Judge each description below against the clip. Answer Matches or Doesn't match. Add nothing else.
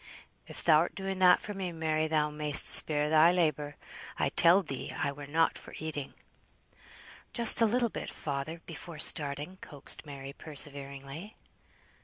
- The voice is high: Doesn't match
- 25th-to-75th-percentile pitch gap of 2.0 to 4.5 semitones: Matches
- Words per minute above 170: Doesn't match